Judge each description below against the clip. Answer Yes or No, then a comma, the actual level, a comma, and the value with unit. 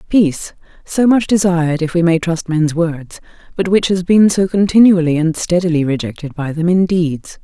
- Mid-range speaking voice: Yes, medium, 170 Hz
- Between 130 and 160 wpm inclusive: No, average, 185 wpm